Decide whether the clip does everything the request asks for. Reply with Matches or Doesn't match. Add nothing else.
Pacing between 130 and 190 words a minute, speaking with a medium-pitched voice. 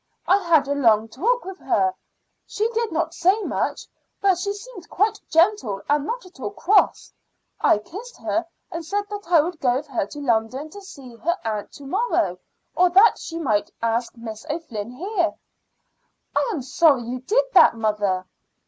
Doesn't match